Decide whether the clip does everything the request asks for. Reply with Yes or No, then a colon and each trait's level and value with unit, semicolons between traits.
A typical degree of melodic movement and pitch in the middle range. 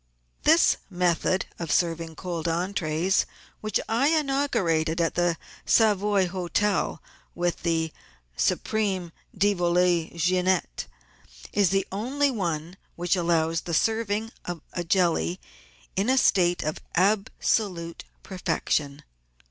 Yes: average, 3.5 semitones; medium, 180 Hz